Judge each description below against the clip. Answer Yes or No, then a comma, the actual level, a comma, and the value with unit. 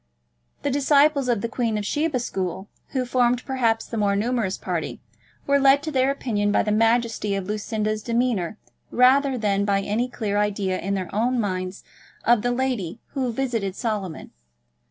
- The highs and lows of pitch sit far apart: No, average, 3.8 semitones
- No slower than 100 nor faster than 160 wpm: No, average, 170 wpm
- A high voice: Yes, high, 230 Hz